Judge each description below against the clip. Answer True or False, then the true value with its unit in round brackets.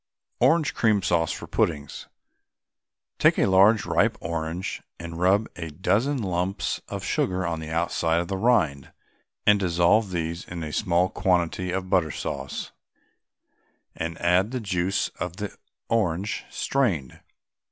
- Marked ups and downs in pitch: False (3.1 semitones)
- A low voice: True (90 Hz)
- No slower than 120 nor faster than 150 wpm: True (140 wpm)